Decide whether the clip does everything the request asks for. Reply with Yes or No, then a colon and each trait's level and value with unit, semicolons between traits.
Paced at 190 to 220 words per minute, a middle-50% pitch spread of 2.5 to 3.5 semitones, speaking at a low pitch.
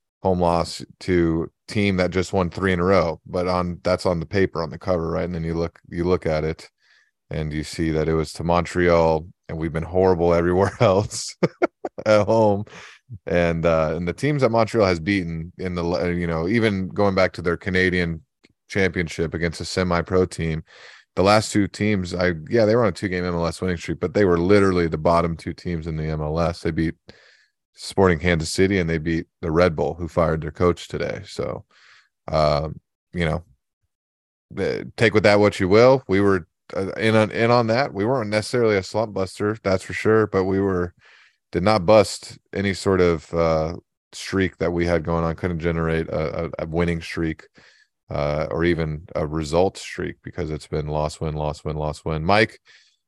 Yes: average, 200 wpm; average, 2.8 semitones; very low, 85 Hz